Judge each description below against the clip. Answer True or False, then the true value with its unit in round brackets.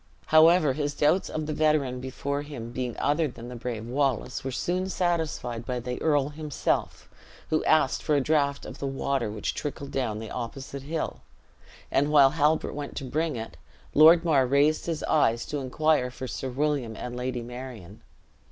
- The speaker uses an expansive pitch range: False (3.5 semitones)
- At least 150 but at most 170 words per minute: False (180 wpm)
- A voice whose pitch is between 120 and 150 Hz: True (140 Hz)